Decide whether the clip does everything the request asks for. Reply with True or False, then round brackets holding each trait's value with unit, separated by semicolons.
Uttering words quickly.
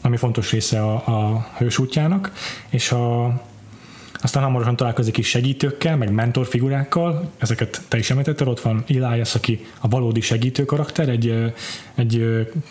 False (140 wpm)